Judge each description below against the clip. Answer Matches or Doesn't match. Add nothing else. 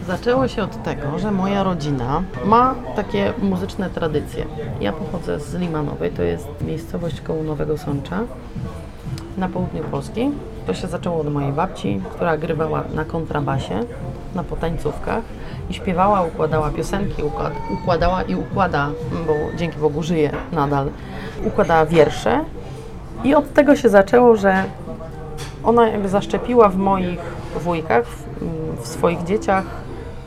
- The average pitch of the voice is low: Doesn't match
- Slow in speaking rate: Doesn't match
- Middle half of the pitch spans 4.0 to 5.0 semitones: Matches